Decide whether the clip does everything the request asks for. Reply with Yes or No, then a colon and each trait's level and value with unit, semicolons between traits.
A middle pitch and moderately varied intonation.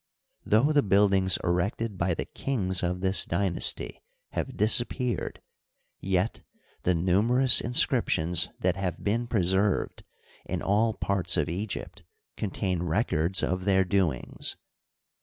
No: very low, 95 Hz; average, 3.0 semitones